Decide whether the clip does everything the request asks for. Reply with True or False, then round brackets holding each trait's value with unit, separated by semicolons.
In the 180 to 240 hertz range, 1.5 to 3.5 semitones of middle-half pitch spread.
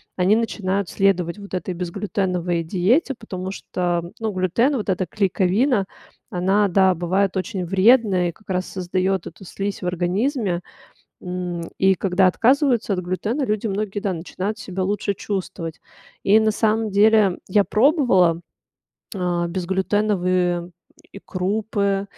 True (190 Hz; 2.7 semitones)